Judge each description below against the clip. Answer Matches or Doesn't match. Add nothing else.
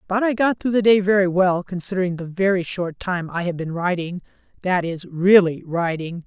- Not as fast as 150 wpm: Doesn't match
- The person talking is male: Doesn't match